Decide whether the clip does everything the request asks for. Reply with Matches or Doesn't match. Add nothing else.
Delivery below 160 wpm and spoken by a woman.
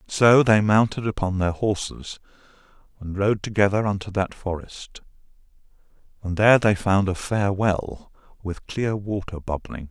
Doesn't match